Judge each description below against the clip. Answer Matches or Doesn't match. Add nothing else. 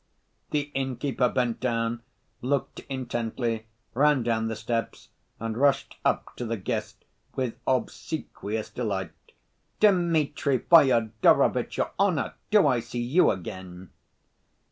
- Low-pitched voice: Matches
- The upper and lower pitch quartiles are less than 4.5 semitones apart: Matches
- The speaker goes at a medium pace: Doesn't match